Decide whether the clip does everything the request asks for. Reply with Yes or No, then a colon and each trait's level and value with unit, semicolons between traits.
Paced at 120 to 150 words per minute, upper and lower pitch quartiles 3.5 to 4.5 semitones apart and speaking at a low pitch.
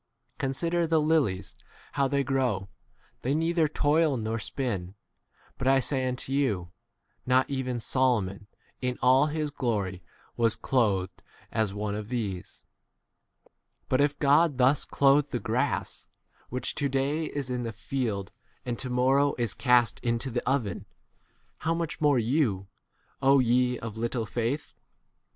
Yes: average, 145 wpm; average, 3.9 semitones; low, 125 Hz